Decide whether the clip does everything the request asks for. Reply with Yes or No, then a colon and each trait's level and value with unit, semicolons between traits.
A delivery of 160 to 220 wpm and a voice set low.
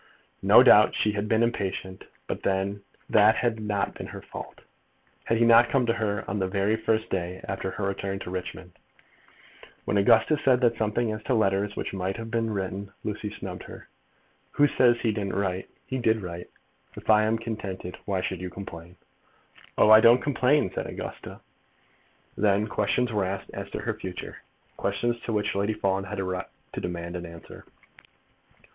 Yes: average, 175 wpm; low, 105 Hz